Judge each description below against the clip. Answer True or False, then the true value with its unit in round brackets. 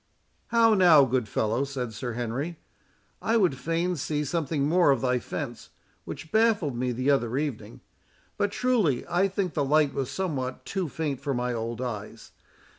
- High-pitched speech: False (140 Hz)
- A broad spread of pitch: True (5.8 semitones)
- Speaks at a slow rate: False (170 wpm)